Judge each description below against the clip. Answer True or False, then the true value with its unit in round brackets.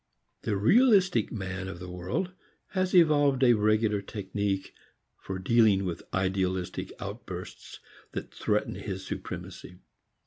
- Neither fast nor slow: False (115 wpm)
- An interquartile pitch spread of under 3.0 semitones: False (5.3 semitones)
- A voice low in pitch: True (100 Hz)